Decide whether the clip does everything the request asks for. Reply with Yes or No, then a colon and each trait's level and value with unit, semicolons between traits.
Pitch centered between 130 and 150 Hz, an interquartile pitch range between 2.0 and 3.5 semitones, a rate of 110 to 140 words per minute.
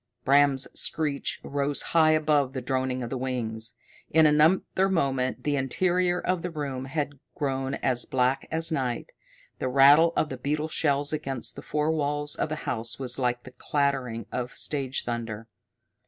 No: medium, 140 Hz; average, 3.0 semitones; average, 165 wpm